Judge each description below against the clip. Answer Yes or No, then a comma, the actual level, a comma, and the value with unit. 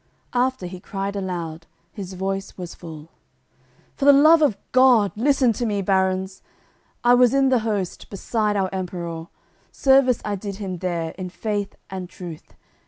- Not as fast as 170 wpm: Yes, average, 160 wpm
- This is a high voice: Yes, high, 195 Hz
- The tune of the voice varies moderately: Yes, average, 4.8 semitones